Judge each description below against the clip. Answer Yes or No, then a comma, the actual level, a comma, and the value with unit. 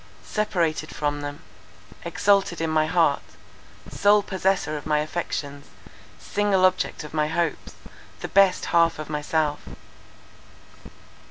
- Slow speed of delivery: Yes, slow, 115 wpm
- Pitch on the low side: No, medium, 165 Hz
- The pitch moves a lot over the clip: No, average, 3.6 semitones